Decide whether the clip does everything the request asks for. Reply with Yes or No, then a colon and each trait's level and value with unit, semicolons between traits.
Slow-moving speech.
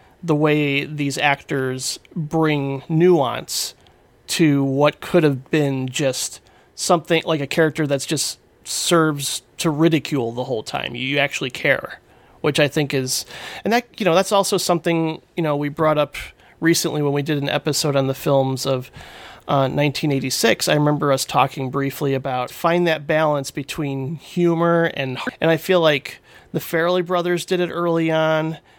No: average, 170 wpm